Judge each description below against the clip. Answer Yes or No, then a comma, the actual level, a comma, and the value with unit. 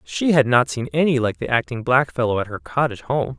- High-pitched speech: No, low, 125 Hz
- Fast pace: Yes, fast, 230 wpm